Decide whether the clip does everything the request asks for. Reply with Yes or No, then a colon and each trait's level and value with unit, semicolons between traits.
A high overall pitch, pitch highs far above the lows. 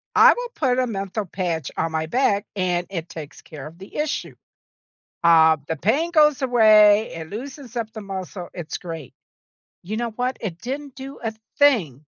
Yes: high, 205 Hz; wide, 7.1 semitones